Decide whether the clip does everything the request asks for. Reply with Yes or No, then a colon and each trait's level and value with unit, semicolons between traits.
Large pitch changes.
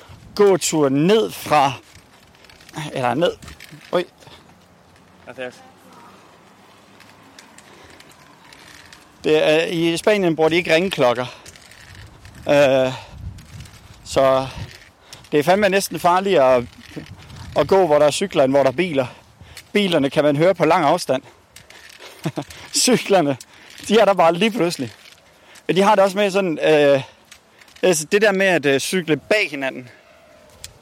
Yes: wide, 6.7 semitones